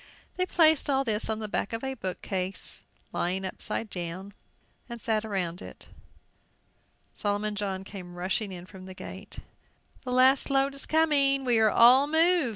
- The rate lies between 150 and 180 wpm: Yes, average, 160 wpm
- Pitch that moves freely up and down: Yes, wide, 6.1 semitones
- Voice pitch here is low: No, high, 215 Hz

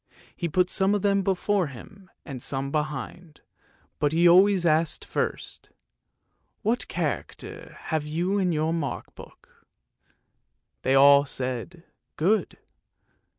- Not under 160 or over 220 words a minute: No, slow, 135 wpm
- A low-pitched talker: No, medium, 165 Hz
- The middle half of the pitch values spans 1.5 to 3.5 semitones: No, average, 4.5 semitones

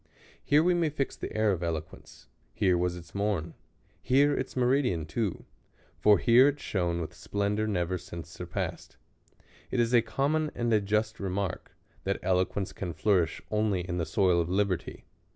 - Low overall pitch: Yes, low, 100 Hz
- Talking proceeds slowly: No, average, 170 wpm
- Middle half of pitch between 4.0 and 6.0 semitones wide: Yes, average, 5.1 semitones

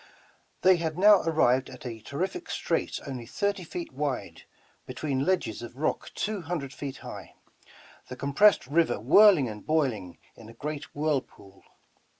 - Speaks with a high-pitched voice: No, medium, 145 Hz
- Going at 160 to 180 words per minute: No, average, 150 wpm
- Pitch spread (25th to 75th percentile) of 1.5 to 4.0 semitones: No, average, 5.2 semitones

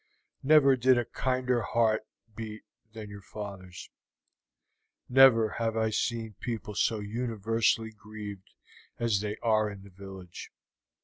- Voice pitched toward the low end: Yes, low, 110 Hz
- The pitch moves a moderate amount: No, narrow, 2.3 semitones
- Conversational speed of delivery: No, slow, 125 wpm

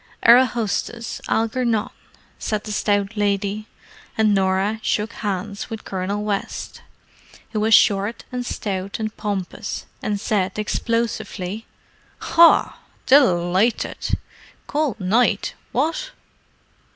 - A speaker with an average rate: No, slow, 105 wpm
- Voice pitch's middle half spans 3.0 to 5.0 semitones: No, narrow, 2.5 semitones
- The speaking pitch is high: Yes, high, 210 Hz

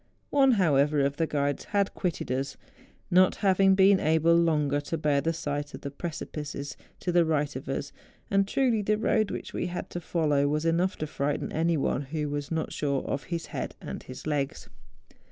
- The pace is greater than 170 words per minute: Yes, average, 195 wpm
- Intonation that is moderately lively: Yes, average, 3.8 semitones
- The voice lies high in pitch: No, medium, 155 Hz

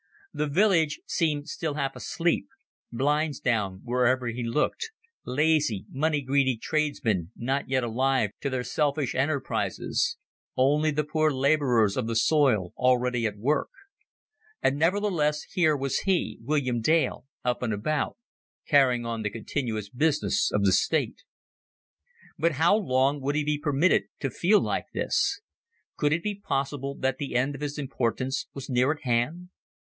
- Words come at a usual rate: Yes, average, 150 wpm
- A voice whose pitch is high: No, medium, 140 Hz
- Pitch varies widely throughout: No, average, 3.6 semitones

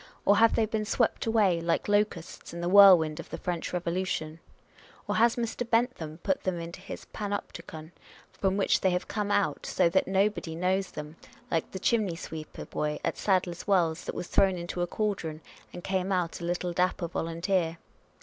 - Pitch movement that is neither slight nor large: Yes, average, 3.2 semitones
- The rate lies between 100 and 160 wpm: No, average, 185 wpm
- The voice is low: No, medium, 180 Hz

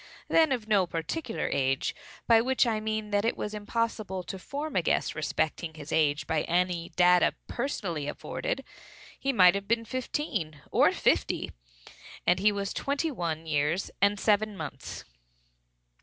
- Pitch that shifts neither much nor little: No, wide, 5.7 semitones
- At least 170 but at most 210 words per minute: No, average, 155 wpm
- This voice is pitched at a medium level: No, high, 200 Hz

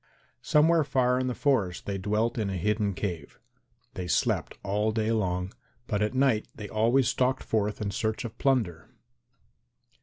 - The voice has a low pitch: Yes, low, 110 Hz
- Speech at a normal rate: Yes, average, 160 wpm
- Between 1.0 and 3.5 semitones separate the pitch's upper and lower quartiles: No, average, 4.0 semitones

